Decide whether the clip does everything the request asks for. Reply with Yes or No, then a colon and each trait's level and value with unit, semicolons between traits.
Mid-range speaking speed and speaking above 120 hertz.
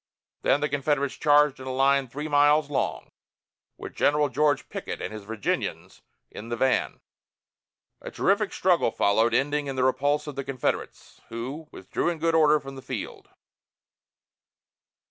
Yes: average, 155 wpm; medium, 140 Hz